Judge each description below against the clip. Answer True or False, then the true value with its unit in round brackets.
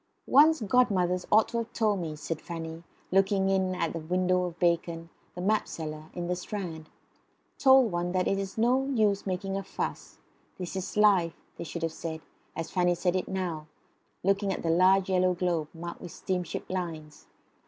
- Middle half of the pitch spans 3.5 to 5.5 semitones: False (2.7 semitones)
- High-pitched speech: False (180 Hz)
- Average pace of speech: True (180 wpm)